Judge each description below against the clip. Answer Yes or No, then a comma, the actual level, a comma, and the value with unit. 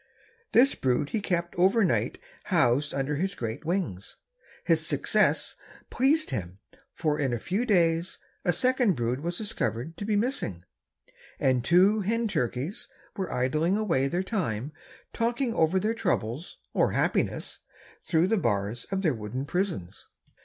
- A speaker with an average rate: Yes, average, 145 wpm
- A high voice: No, medium, 170 Hz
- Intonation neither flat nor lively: No, wide, 8.0 semitones